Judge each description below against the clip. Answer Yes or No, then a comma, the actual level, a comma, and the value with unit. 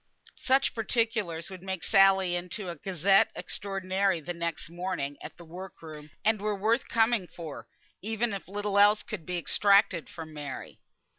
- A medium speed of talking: Yes, average, 160 wpm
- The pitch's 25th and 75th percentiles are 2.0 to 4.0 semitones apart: Yes, average, 3.4 semitones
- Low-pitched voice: No, high, 190 Hz